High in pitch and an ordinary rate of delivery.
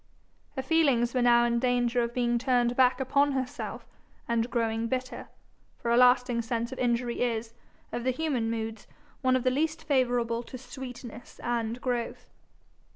Yes: high, 245 Hz; average, 160 wpm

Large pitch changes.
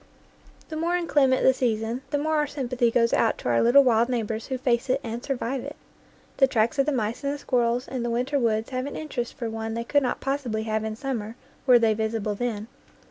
No: average, 3.3 semitones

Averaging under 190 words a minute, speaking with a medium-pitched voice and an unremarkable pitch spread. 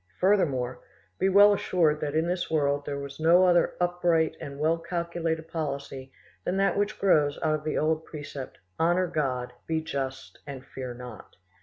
Yes: average, 170 wpm; medium, 155 Hz; average, 3.7 semitones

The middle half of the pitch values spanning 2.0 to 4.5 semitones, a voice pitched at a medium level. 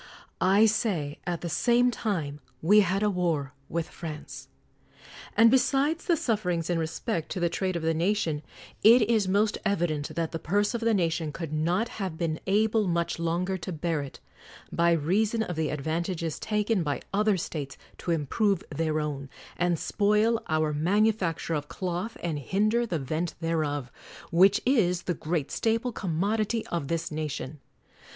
No: average, 4.9 semitones; medium, 175 Hz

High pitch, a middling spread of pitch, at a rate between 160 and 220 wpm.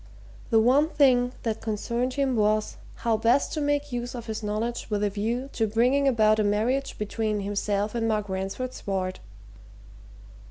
Yes: high, 225 Hz; average, 3.1 semitones; average, 165 wpm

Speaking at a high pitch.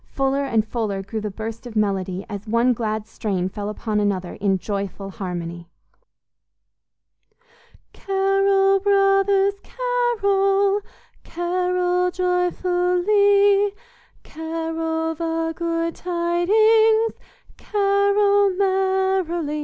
Yes: very high, 345 Hz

